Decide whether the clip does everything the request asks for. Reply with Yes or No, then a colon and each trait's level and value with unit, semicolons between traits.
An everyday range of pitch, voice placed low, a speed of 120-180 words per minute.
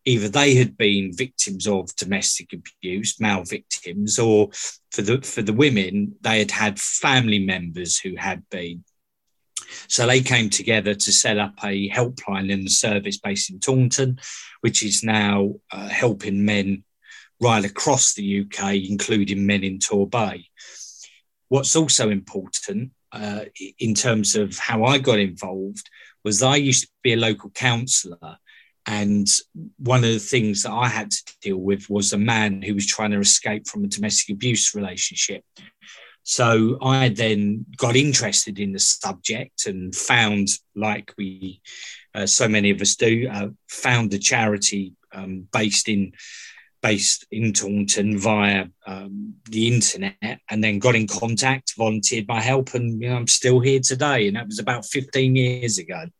Yes: average, 3.7 semitones; low, 105 Hz; average, 160 wpm